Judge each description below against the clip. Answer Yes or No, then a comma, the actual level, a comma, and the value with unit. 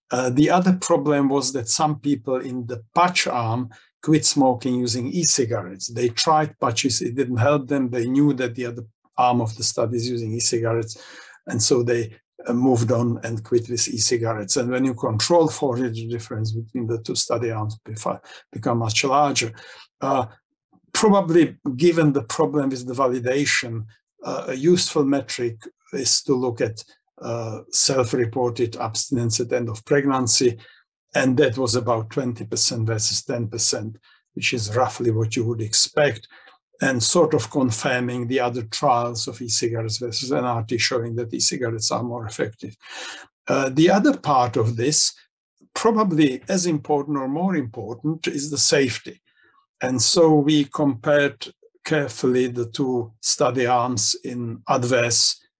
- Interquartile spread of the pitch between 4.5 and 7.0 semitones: No, average, 3.6 semitones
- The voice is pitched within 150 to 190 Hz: No, low, 125 Hz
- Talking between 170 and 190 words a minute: No, average, 155 wpm